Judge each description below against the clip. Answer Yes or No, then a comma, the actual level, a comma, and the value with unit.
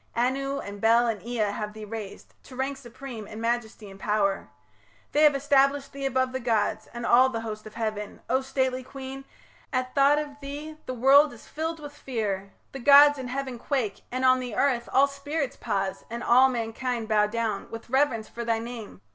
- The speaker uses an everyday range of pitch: Yes, average, 3.7 semitones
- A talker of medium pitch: No, very high, 250 Hz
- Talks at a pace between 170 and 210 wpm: Yes, average, 195 wpm